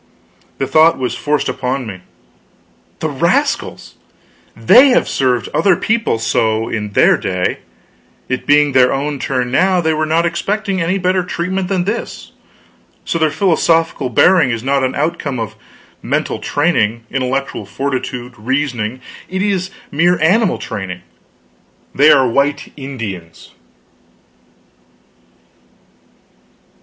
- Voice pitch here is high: No, medium, 140 Hz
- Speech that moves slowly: Yes, slow, 125 wpm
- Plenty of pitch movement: Yes, wide, 5.9 semitones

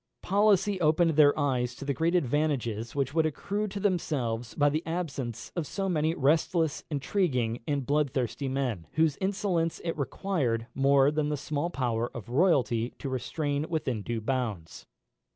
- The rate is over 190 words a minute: No, average, 155 wpm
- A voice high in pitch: No, medium, 145 Hz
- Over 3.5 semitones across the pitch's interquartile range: Yes, average, 4.9 semitones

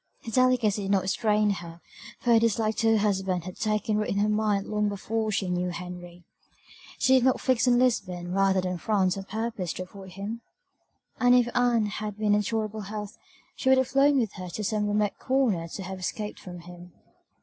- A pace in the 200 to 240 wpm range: Yes, fast, 205 wpm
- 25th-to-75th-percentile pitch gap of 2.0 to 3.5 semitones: Yes, average, 3.2 semitones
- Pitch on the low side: No, high, 210 Hz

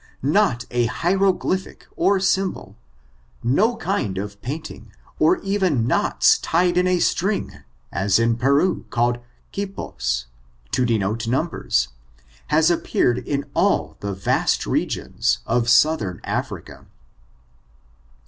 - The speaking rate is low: Yes, slow, 120 wpm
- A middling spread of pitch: No, wide, 8.3 semitones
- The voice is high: No, low, 135 Hz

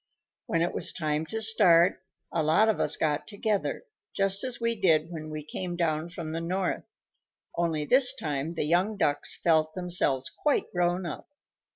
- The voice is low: No, medium, 170 Hz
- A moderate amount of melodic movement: Yes, average, 3.8 semitones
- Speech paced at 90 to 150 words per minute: No, average, 175 wpm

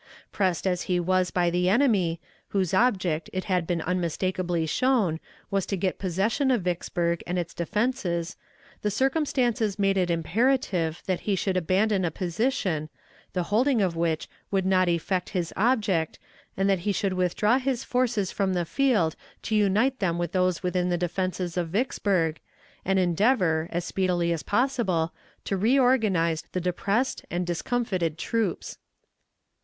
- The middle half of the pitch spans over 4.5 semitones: No, average, 3.6 semitones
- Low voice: No, medium, 185 Hz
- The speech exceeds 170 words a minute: No, average, 155 wpm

